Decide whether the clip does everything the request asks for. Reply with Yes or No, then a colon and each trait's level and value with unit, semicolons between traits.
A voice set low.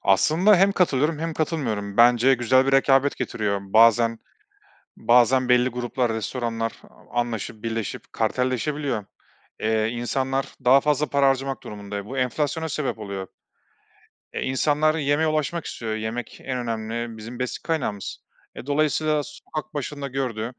Yes: low, 125 Hz